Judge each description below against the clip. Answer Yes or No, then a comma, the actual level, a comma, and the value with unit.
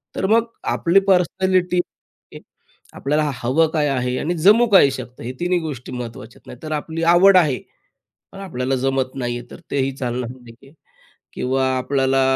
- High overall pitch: No, medium, 140 Hz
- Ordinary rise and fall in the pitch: No, wide, 5.7 semitones